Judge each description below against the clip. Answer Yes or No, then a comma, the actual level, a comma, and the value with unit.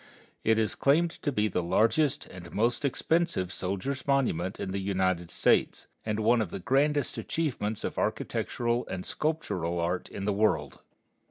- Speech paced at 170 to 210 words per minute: No, average, 160 wpm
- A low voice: Yes, low, 110 Hz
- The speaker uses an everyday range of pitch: No, wide, 6.9 semitones